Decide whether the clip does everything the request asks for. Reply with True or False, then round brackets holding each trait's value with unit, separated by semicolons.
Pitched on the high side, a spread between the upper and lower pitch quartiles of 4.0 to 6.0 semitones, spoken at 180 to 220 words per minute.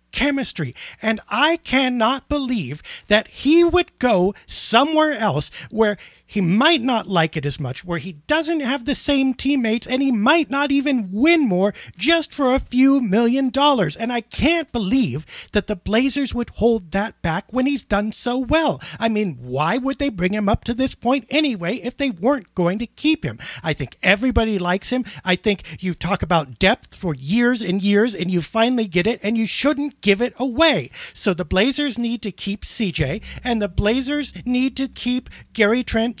True (235 Hz; 5.3 semitones; 190 wpm)